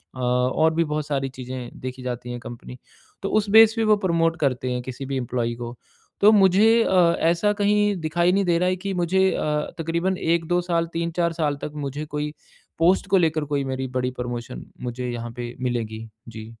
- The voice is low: No, medium, 155 Hz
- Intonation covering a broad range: Yes, wide, 6.2 semitones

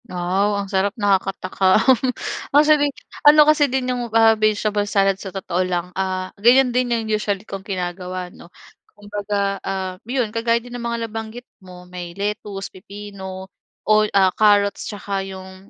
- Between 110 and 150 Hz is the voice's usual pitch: No, high, 200 Hz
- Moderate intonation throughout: Yes, average, 3.2 semitones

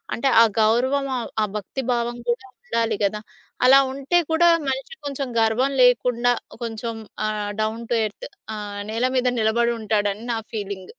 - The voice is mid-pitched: No, high, 230 Hz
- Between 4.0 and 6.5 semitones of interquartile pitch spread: No, average, 2.9 semitones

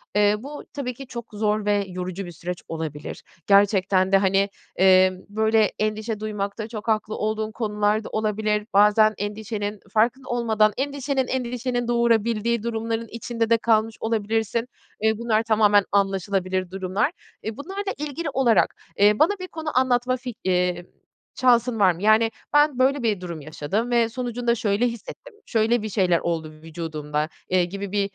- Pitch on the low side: No, high, 215 Hz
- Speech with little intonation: No, average, 3.1 semitones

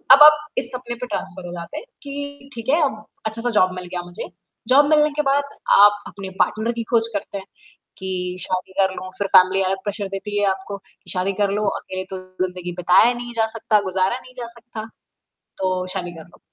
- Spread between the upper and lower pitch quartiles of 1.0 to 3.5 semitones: No, average, 4.4 semitones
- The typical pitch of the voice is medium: No, high, 205 Hz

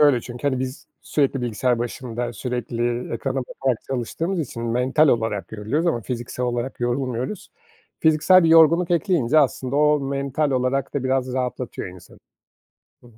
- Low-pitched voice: Yes, low, 130 Hz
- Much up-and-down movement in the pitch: No, average, 3.2 semitones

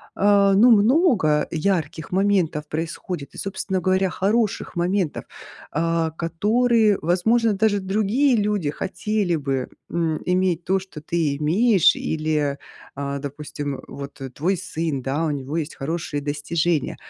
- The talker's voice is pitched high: No, medium, 170 Hz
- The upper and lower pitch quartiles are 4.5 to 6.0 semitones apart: Yes, average, 4.8 semitones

